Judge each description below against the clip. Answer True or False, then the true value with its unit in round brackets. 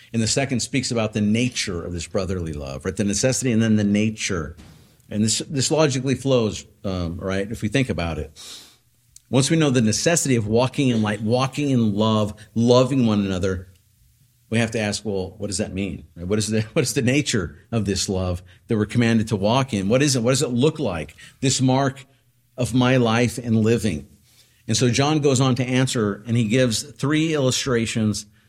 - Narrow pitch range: False (3.9 semitones)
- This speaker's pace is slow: False (205 wpm)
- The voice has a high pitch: False (115 Hz)